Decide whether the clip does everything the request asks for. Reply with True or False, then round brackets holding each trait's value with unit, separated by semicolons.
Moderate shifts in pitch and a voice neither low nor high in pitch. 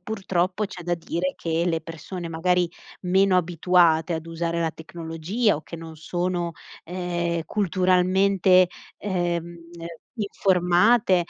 False (1.8 semitones; 175 Hz)